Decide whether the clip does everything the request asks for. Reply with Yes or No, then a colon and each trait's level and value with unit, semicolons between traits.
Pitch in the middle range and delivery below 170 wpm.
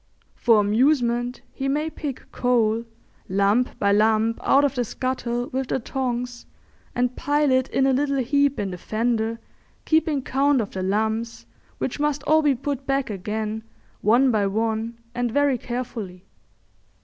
No: high, 245 Hz; average, 155 wpm